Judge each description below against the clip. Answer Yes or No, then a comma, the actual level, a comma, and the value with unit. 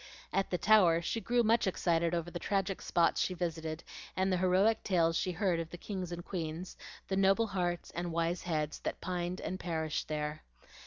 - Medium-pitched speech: Yes, medium, 175 Hz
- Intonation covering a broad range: No, narrow, 2.4 semitones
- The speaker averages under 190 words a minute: No, average, 195 wpm